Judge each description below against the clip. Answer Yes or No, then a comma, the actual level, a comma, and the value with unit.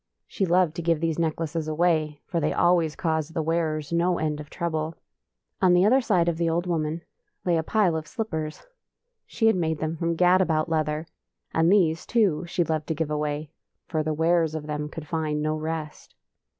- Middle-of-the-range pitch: Yes, medium, 160 Hz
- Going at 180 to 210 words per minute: Yes, average, 200 wpm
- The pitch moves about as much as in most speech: No, narrow, 1.9 semitones